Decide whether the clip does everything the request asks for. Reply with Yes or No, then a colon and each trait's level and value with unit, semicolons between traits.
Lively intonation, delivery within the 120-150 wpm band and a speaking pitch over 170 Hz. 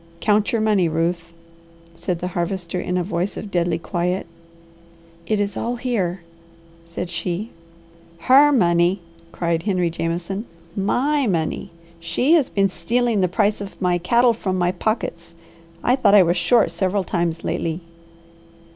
No: average, 3.8 semitones; average, 145 wpm; medium, 185 Hz